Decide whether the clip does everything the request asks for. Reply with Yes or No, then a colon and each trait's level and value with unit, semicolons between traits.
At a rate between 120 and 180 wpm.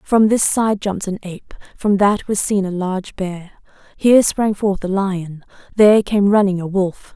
No: average, 195 wpm